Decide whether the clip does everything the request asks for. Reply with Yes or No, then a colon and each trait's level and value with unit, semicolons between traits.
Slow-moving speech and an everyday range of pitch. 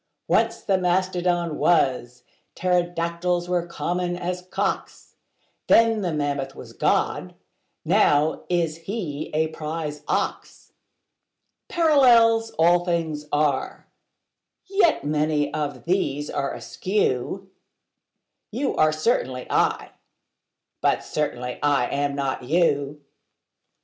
Yes: slow, 100 wpm; average, 3.7 semitones